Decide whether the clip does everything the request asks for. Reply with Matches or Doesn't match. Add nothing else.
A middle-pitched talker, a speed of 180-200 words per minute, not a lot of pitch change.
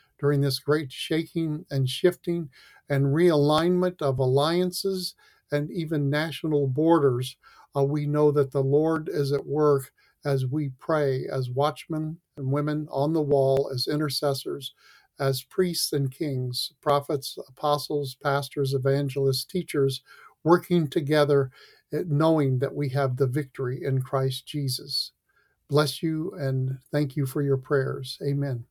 Doesn't match